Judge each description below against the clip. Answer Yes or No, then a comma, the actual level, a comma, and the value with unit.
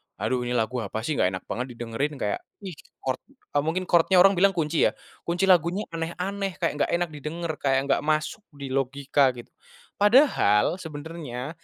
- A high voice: No, medium, 155 Hz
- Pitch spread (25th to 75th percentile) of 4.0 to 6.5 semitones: Yes, average, 5.1 semitones